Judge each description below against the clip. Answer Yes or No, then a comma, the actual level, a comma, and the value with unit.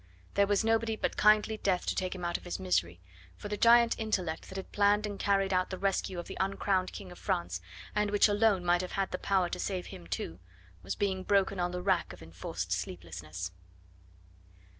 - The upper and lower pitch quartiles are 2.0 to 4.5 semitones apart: Yes, average, 2.9 semitones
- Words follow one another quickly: Yes, fast, 210 wpm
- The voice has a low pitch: No, high, 190 Hz